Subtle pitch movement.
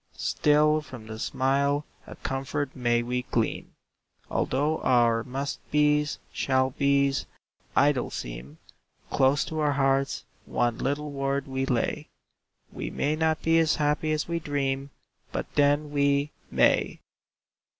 Yes: narrow, 2.2 semitones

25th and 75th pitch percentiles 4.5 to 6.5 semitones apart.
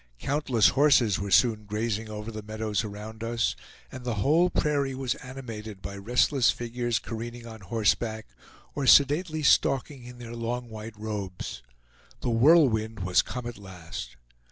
No: average, 2.9 semitones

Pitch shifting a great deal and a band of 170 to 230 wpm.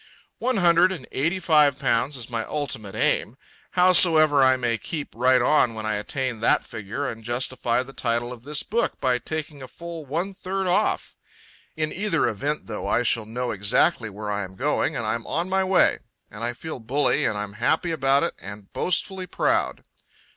Yes: wide, 5.9 semitones; average, 190 wpm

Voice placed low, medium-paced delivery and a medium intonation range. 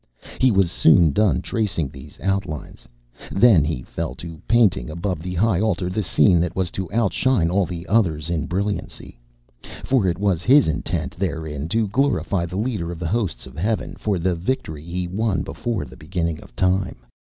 Yes: very low, 90 Hz; average, 180 wpm; average, 4.0 semitones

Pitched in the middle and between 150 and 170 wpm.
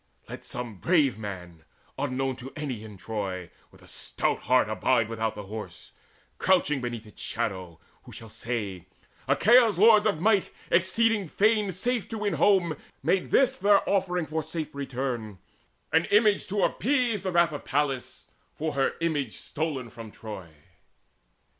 Yes: medium, 145 Hz; average, 155 wpm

